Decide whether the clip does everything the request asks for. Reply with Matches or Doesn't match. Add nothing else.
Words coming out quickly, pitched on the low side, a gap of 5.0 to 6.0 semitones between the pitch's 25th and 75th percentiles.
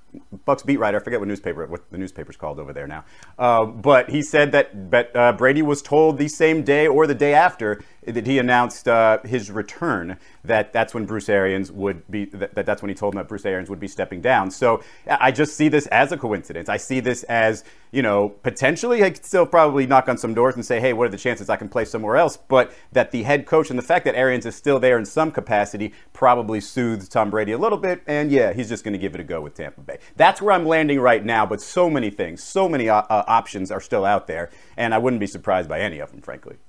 Matches